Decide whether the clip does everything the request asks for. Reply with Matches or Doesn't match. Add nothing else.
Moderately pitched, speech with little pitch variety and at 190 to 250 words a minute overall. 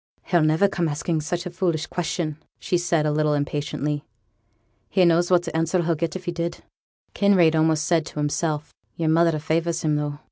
Matches